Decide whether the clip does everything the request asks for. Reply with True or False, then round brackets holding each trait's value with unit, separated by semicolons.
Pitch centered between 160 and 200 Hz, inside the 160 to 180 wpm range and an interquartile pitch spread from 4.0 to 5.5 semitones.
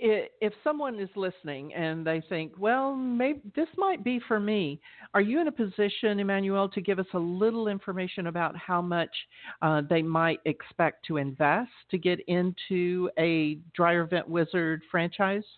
True (185 Hz; 165 wpm; 4.4 semitones)